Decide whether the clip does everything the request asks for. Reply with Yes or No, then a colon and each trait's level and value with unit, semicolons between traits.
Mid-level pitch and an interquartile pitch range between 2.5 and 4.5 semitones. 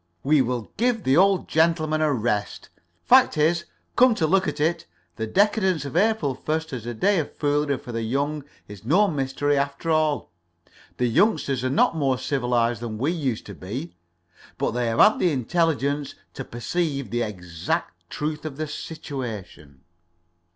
No: medium, 145 Hz; average, 5.1 semitones